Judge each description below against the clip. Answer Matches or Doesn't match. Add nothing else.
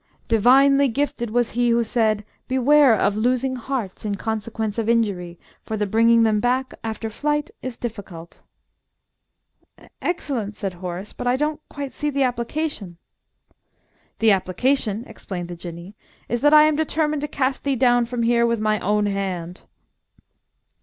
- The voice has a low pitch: Doesn't match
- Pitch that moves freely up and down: Doesn't match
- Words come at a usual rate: Matches